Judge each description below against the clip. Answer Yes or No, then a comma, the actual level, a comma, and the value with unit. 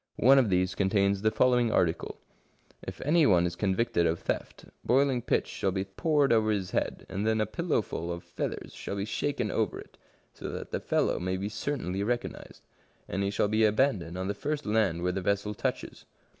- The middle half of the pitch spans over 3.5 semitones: Yes, average, 4.3 semitones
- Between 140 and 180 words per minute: No, fast, 205 wpm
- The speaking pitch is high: No, low, 105 Hz